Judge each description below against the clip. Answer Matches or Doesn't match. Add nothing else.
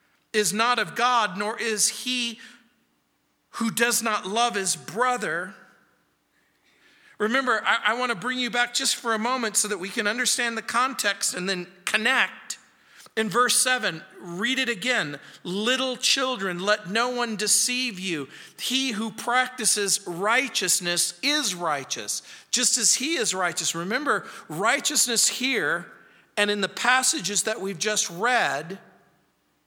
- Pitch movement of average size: Matches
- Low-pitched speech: Doesn't match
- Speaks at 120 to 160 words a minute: Matches